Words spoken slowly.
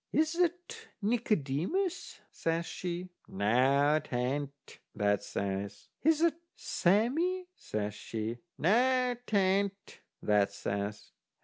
Yes: slow, 95 wpm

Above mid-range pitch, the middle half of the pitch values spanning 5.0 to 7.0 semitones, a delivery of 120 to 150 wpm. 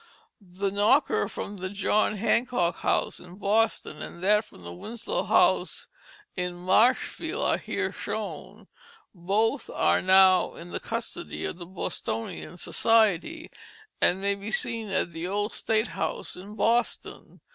No: high, 200 Hz; average, 3.7 semitones; average, 140 wpm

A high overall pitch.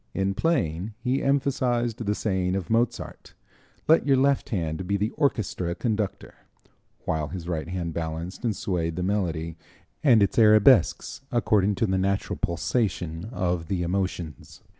No: very low, 95 Hz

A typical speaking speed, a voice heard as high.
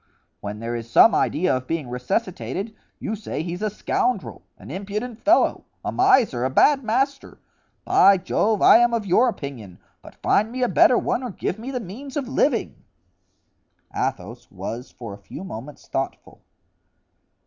Yes: average, 165 wpm; high, 200 Hz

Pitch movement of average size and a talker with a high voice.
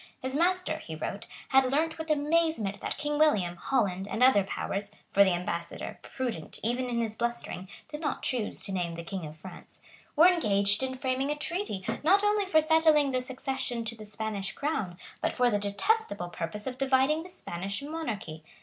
No: wide, 7.0 semitones; very high, 250 Hz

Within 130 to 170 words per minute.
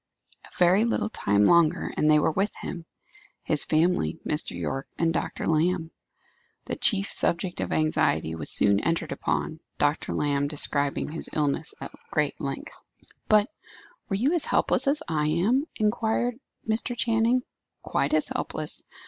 Yes: average, 150 wpm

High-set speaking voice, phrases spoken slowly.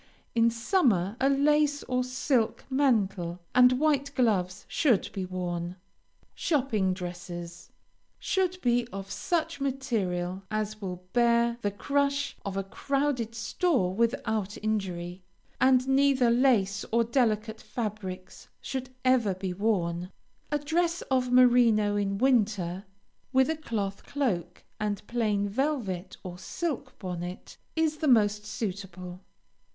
Yes: high, 225 Hz; slow, 125 wpm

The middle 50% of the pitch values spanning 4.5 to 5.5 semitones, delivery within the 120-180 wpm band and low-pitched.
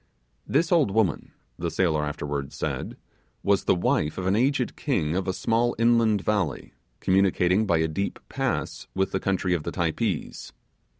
Yes: average, 4.8 semitones; average, 165 wpm; very low, 95 Hz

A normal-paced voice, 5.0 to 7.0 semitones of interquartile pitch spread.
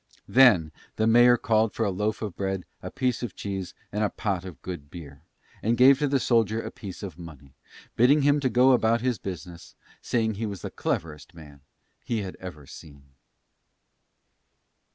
Yes: average, 180 wpm; wide, 5.6 semitones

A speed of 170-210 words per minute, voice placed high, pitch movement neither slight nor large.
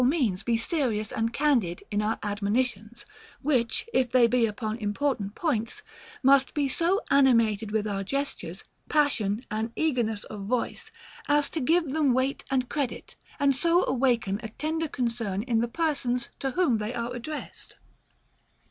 No: average, 160 wpm; high, 245 Hz; average, 4.4 semitones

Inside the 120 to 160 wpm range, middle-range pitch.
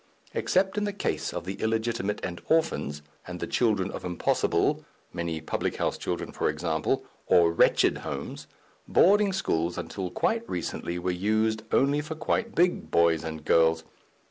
No: average, 150 wpm; very low, 95 Hz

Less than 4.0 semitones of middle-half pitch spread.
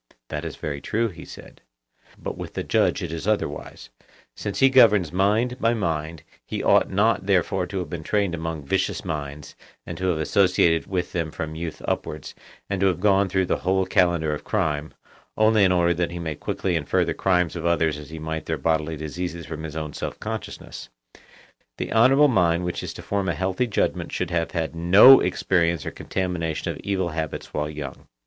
Yes: average, 3.5 semitones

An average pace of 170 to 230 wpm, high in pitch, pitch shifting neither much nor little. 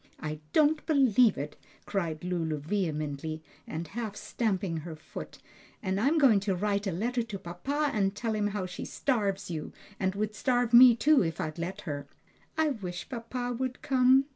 No: average, 175 wpm; high, 205 Hz; wide, 6.1 semitones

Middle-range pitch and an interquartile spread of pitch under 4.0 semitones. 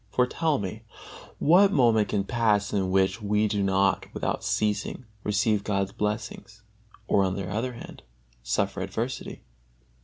No: low, 105 Hz; average, 2.8 semitones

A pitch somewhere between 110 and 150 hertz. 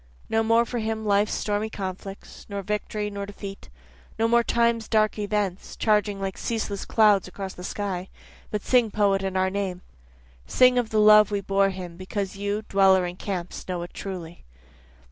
No: high, 200 Hz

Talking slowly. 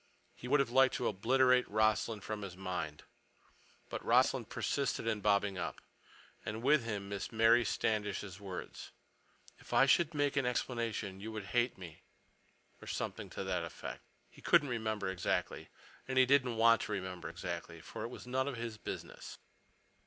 No: average, 165 wpm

